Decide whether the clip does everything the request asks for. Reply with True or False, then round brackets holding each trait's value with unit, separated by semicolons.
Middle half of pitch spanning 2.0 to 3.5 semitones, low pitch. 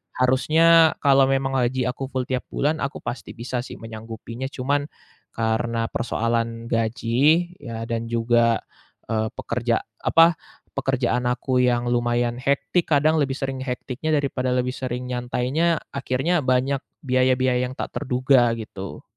True (2.4 semitones; 125 Hz)